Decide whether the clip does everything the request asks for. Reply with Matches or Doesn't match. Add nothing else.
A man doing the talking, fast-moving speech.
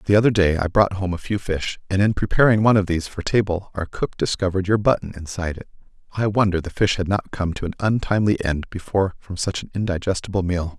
Matches